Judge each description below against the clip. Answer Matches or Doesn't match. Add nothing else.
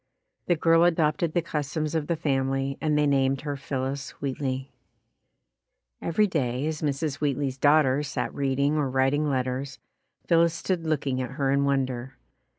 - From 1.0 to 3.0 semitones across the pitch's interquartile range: Matches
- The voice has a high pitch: Doesn't match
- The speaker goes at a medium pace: Matches